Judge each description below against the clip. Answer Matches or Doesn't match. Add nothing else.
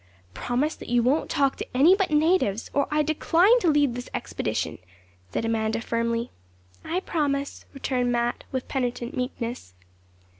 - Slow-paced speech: Doesn't match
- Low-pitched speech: Doesn't match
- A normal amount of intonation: Matches